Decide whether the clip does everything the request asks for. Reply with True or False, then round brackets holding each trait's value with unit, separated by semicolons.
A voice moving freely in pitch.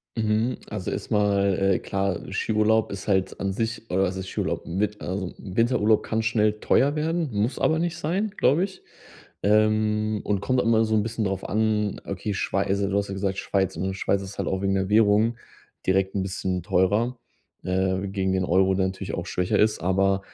False (2.4 semitones)